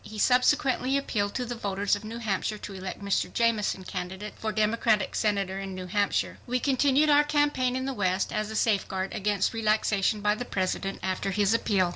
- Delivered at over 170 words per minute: Yes, average, 190 wpm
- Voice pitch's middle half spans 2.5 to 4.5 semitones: Yes, average, 3.6 semitones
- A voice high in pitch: Yes, high, 210 Hz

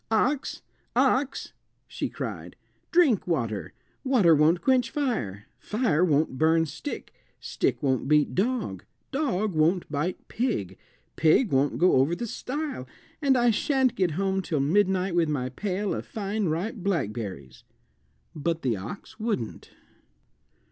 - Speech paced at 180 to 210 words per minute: No, slow, 135 wpm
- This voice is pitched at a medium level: Yes, medium, 180 Hz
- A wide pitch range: Yes, wide, 7.9 semitones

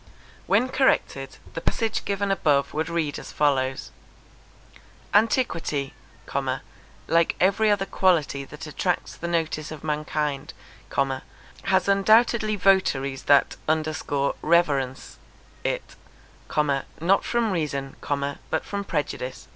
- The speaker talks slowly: Yes, slow, 100 wpm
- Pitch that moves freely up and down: Yes, wide, 5.7 semitones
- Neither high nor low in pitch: Yes, medium, 160 Hz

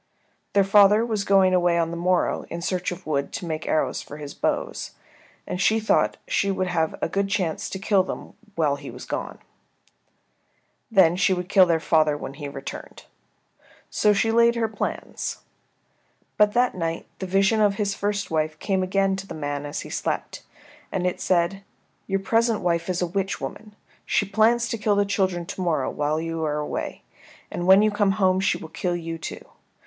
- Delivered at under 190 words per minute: No, average, 195 wpm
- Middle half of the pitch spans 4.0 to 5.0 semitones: No, average, 3.5 semitones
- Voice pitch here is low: No, medium, 185 Hz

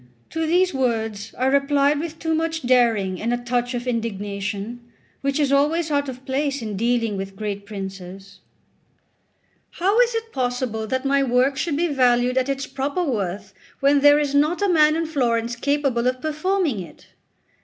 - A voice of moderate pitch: No, very high, 260 Hz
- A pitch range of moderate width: Yes, average, 4.5 semitones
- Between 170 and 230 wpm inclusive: Yes, average, 175 wpm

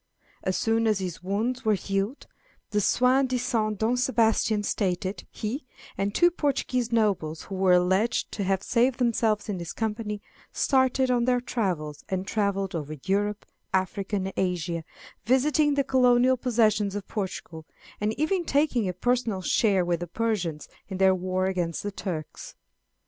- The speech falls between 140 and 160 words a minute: Yes, average, 155 wpm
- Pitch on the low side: No, high, 210 Hz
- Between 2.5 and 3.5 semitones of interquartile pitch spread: No, average, 4.6 semitones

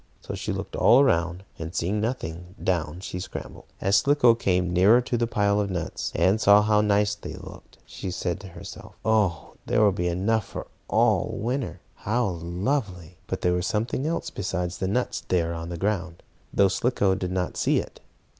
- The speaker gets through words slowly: No, average, 190 wpm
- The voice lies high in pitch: No, very low, 95 Hz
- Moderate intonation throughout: Yes, average, 3.4 semitones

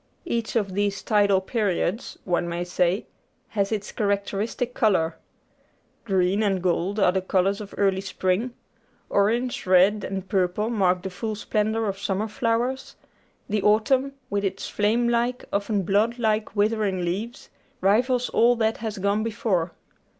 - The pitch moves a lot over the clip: No, average, 2.8 semitones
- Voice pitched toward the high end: Yes, high, 205 Hz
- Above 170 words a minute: No, average, 145 wpm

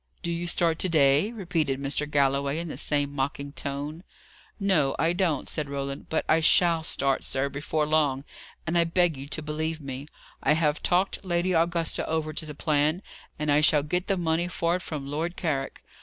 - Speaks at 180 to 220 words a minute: Yes, average, 195 wpm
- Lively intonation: No, average, 3.1 semitones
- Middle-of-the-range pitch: Yes, medium, 155 Hz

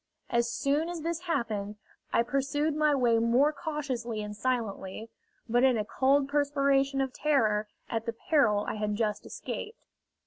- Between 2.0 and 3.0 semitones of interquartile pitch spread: No, average, 4.3 semitones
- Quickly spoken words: No, average, 160 wpm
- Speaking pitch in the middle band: No, very high, 255 Hz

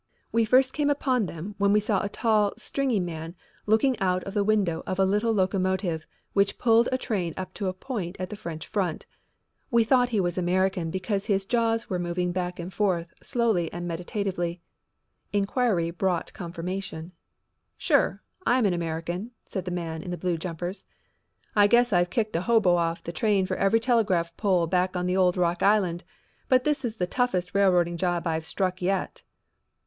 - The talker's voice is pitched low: No, medium, 185 Hz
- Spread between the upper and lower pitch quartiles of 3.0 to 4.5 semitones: Yes, average, 3.5 semitones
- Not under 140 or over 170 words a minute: No, average, 185 wpm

